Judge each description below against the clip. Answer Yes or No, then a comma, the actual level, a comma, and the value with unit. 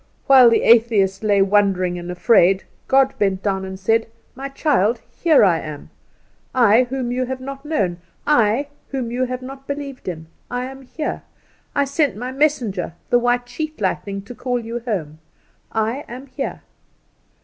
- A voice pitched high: Yes, high, 240 Hz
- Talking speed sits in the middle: Yes, average, 165 wpm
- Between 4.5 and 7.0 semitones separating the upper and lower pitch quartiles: Yes, average, 5.3 semitones